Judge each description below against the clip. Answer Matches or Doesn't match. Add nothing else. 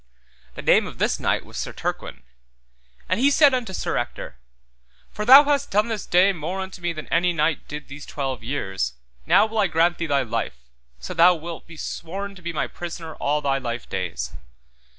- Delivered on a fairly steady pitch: Doesn't match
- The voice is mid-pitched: Matches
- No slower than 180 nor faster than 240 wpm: Matches